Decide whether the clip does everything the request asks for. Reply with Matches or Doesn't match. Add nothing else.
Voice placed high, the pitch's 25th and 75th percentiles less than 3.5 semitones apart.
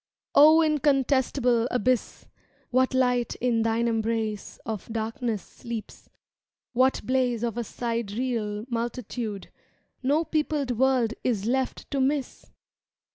Matches